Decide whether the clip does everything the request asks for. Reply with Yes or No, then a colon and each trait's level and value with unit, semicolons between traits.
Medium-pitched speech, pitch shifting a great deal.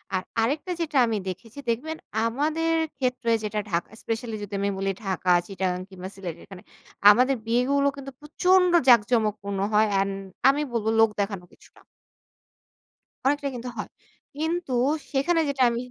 No: high, 235 Hz; wide, 5.9 semitones